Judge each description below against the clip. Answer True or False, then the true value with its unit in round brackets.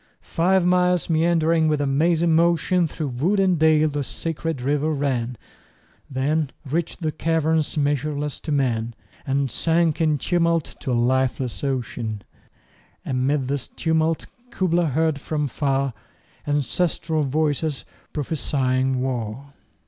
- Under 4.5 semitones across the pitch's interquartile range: True (3.4 semitones)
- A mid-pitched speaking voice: True (150 Hz)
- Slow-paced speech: True (130 wpm)